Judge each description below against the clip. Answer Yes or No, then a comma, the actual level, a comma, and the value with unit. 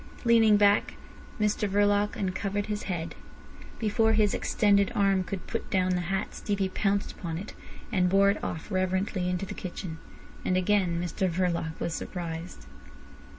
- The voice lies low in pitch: No, high, 195 Hz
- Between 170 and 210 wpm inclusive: No, average, 150 wpm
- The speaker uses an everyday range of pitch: No, narrow, 2.3 semitones